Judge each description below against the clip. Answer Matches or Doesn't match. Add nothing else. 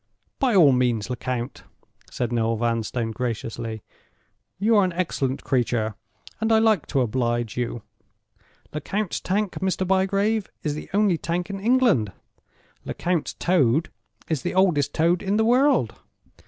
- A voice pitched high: Doesn't match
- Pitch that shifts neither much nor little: Doesn't match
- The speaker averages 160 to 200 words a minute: Doesn't match